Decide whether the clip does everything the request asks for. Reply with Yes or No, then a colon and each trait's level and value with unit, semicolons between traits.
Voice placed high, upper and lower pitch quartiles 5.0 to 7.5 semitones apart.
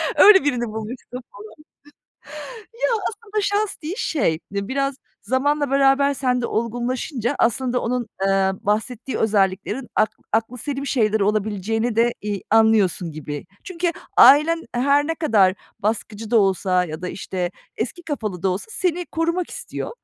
Yes: high, 240 Hz; wide, 5.6 semitones